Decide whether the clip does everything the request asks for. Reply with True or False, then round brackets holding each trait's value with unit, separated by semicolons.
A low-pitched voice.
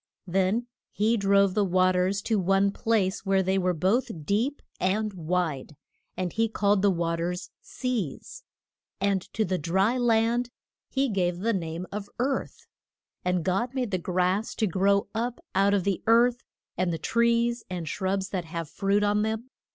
False (195 Hz)